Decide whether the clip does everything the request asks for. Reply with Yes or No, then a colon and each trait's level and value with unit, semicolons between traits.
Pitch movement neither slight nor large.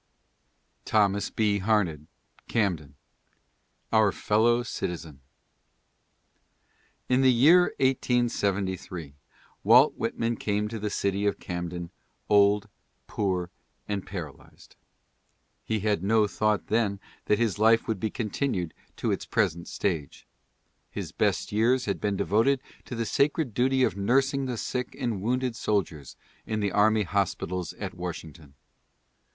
Yes: average, 3.9 semitones